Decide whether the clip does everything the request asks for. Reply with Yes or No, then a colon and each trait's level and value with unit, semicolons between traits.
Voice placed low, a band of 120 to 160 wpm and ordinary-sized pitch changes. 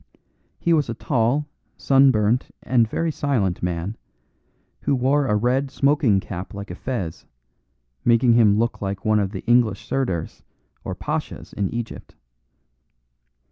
Yes: low, 115 Hz; average, 140 wpm; average, 4.9 semitones